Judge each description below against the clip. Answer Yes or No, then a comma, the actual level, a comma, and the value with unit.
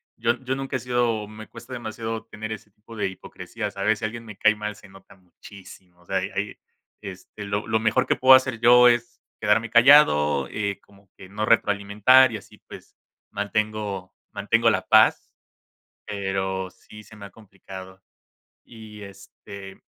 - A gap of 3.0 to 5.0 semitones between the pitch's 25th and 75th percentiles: No, narrow, 2.6 semitones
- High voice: No, low, 105 Hz